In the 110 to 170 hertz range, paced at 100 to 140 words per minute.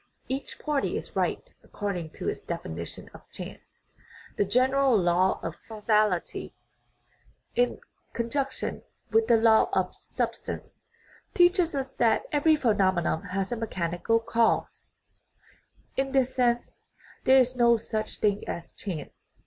No: high, 230 Hz; slow, 135 wpm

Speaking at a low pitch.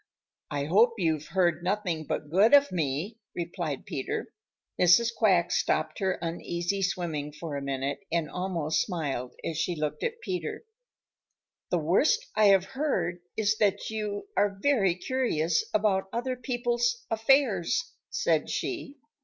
No: high, 190 Hz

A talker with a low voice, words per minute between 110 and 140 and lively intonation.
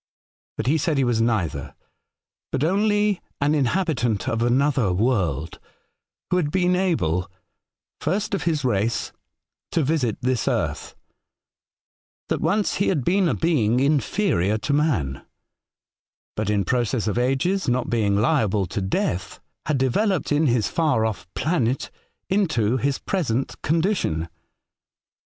Yes: low, 130 Hz; slow, 135 wpm; wide, 7.0 semitones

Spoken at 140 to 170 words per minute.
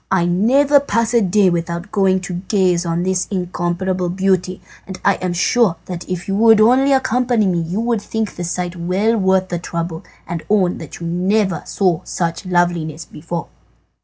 No: average, 180 wpm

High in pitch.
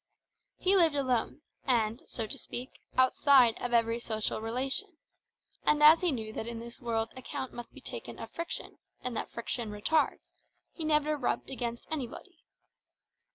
Yes: very high, 250 Hz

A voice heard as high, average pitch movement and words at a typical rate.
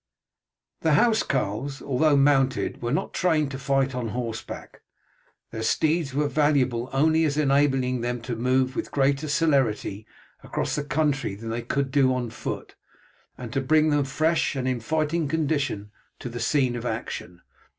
No: low, 135 Hz; average, 3.4 semitones; average, 160 wpm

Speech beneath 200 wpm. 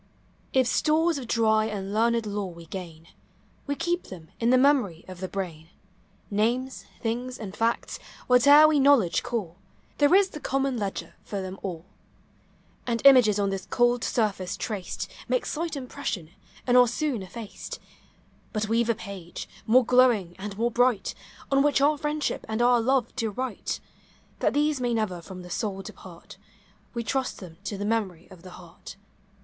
Yes: average, 175 wpm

